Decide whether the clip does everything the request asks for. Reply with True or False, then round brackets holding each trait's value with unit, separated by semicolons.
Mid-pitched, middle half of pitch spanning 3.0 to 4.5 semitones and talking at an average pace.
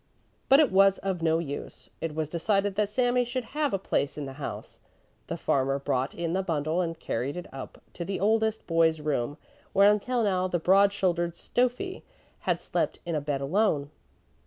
False (180 Hz; 5.3 semitones; 190 wpm)